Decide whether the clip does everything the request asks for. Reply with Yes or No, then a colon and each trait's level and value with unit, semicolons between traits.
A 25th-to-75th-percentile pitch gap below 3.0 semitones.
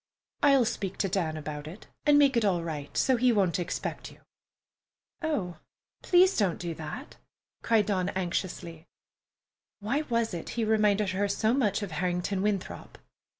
No: average, 4.7 semitones